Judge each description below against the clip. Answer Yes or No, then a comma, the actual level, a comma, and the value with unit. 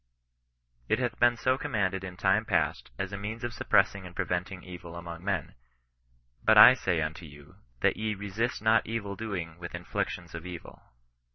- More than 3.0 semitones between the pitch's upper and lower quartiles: Yes, average, 4.2 semitones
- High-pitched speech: No, very low, 95 Hz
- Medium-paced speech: Yes, average, 180 wpm